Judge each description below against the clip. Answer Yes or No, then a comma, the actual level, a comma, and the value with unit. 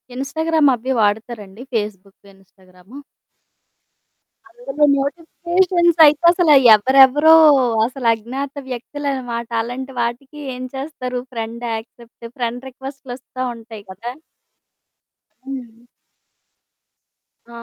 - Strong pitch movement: No, average, 3.6 semitones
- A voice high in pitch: Yes, very high, 255 Hz